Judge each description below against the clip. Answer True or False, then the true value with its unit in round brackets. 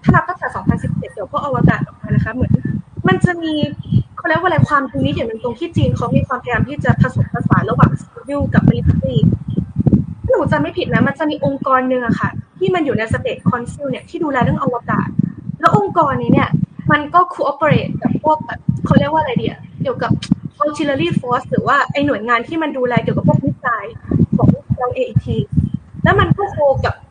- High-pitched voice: True (285 Hz)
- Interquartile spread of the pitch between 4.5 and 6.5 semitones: True (4.9 semitones)